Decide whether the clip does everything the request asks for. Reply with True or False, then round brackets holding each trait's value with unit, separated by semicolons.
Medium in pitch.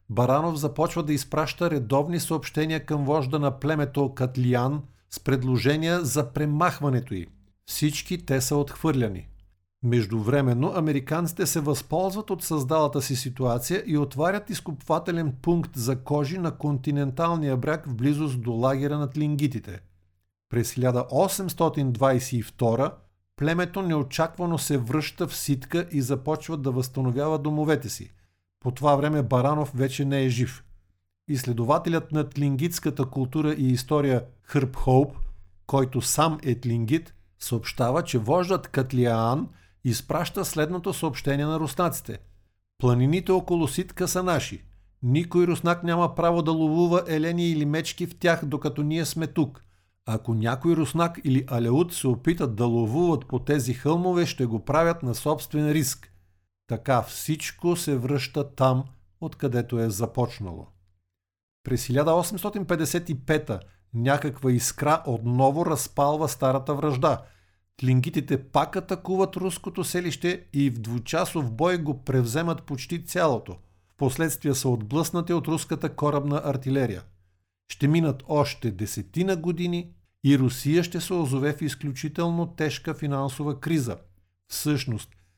True (145 Hz)